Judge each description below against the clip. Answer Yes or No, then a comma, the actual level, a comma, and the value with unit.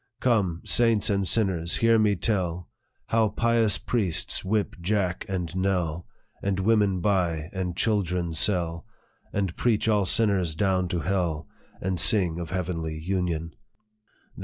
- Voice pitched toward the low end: Yes, very low, 95 Hz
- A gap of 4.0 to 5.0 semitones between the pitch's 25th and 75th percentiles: No, average, 3.3 semitones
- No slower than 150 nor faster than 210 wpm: No, slow, 135 wpm